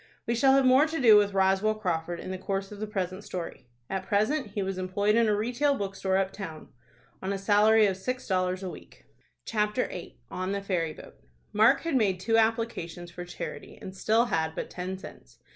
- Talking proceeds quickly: Yes, fast, 210 wpm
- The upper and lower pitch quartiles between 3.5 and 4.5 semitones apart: No, average, 3.1 semitones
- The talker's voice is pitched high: Yes, high, 200 Hz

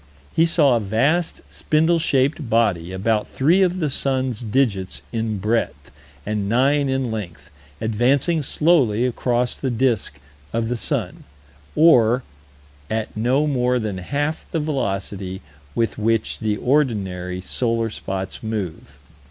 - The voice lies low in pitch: Yes, low, 115 Hz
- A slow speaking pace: Yes, slow, 130 wpm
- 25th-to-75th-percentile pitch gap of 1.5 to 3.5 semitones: No, average, 4.7 semitones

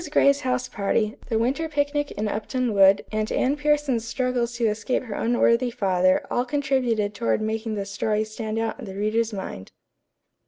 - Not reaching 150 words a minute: No, average, 170 wpm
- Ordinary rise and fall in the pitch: Yes, average, 3.2 semitones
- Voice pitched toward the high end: Yes, high, 230 Hz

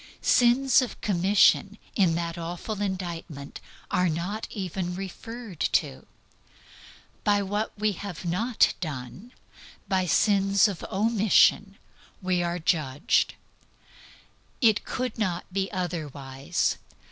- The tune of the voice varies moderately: Yes, average, 3.5 semitones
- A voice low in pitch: No, high, 190 Hz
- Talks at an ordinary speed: No, slow, 105 wpm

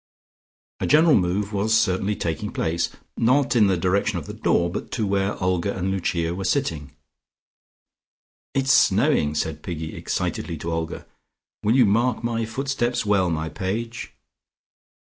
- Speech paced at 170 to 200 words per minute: No, average, 145 wpm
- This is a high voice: No, low, 100 Hz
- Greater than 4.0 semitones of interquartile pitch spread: Yes, average, 5.1 semitones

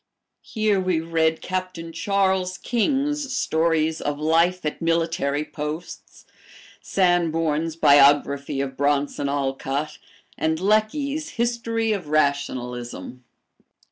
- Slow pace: Yes, slow, 95 wpm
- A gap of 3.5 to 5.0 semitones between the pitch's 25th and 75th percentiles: Yes, average, 4.6 semitones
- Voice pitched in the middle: Yes, medium, 165 Hz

